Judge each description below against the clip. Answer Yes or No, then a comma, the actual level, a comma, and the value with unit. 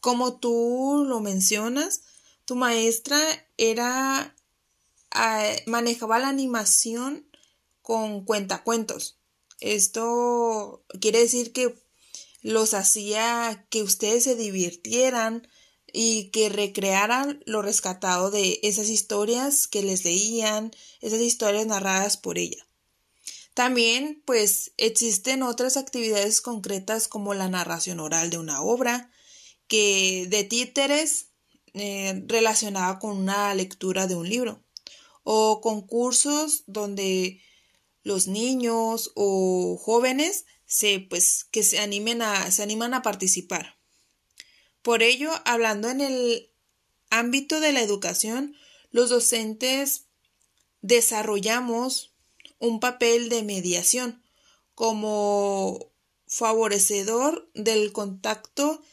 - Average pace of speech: No, slow, 100 wpm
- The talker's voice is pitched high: Yes, high, 225 Hz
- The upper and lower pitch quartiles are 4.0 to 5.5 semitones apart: No, average, 3.2 semitones